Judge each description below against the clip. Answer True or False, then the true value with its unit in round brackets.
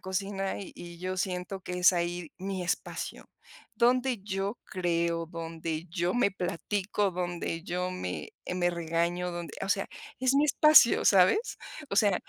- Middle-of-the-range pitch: True (180 Hz)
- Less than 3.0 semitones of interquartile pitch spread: True (2.4 semitones)